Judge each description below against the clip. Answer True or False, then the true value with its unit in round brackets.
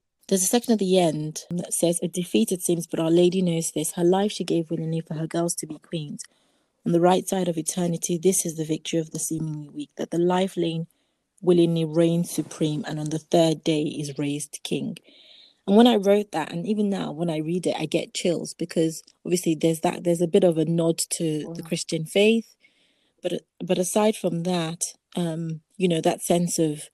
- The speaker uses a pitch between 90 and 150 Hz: False (170 Hz)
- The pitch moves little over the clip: True (2.2 semitones)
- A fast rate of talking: True (215 wpm)